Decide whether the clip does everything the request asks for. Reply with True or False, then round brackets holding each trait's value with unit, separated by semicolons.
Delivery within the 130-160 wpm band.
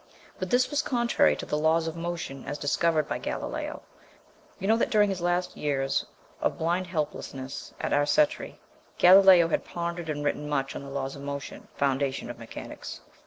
False (180 wpm)